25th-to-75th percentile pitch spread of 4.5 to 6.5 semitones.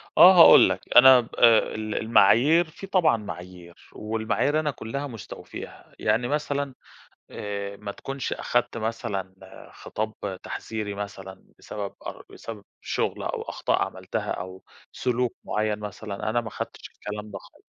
No: average, 3.6 semitones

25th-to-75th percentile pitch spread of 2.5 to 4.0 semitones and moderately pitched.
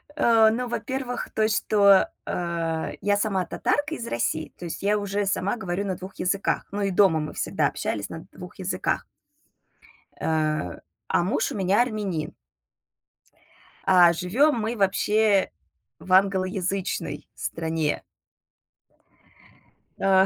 No: average, 3.5 semitones; high, 195 Hz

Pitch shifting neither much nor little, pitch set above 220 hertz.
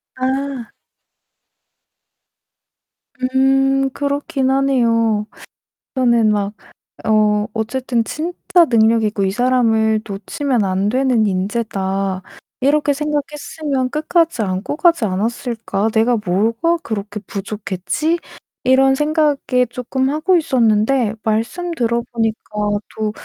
Yes: average, 4.2 semitones; high, 240 Hz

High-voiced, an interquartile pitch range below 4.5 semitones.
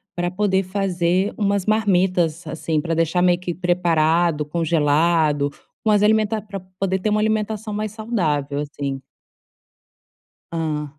No: medium, 180 Hz; average, 4.1 semitones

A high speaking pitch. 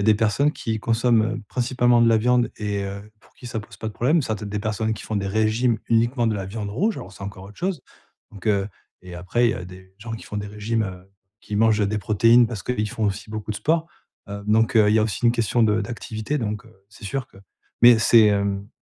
No: low, 110 Hz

